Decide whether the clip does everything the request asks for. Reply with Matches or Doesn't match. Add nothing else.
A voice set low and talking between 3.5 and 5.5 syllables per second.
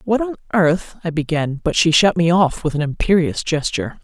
Doesn't match